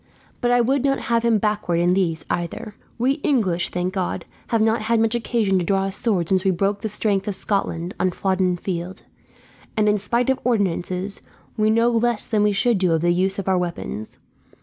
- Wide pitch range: No, average, 3.9 semitones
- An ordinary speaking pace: No, fast, 210 wpm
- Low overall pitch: No, high, 200 Hz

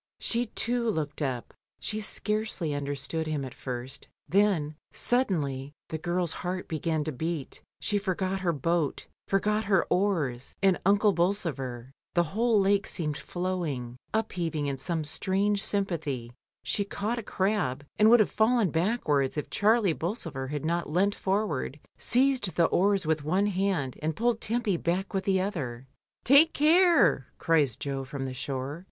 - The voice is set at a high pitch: No, medium, 175 Hz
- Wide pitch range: Yes, wide, 5.8 semitones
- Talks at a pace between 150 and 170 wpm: Yes, average, 155 wpm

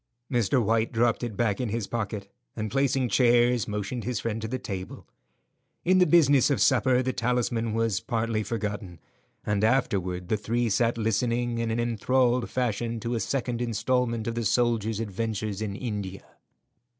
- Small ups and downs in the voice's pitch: Yes, narrow, 2.3 semitones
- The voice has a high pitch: No, low, 115 Hz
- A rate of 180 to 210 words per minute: No, average, 165 wpm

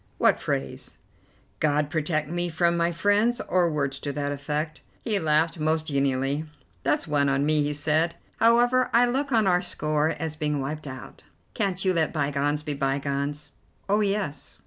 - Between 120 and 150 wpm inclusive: No, average, 170 wpm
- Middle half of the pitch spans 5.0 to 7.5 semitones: No, average, 3.6 semitones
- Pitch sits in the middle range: Yes, medium, 155 Hz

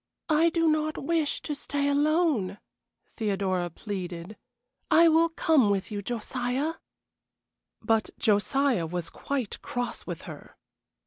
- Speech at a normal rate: No, slow, 120 wpm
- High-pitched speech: Yes, high, 245 Hz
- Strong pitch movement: Yes, wide, 7.3 semitones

